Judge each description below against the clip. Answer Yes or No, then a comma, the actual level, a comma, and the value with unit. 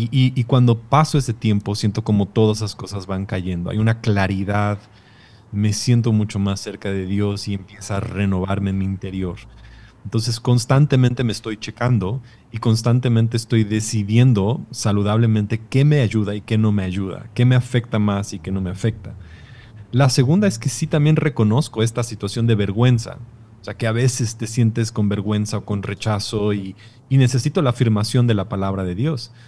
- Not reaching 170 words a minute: No, average, 185 wpm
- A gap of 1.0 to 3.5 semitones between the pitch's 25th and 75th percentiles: Yes, average, 3.0 semitones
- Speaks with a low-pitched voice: Yes, low, 110 Hz